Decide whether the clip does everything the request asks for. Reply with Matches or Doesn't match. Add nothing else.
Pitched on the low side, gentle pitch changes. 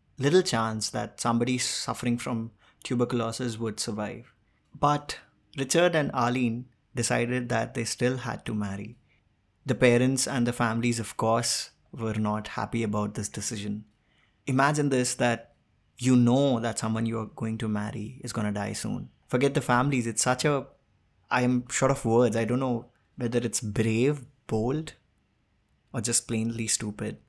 Matches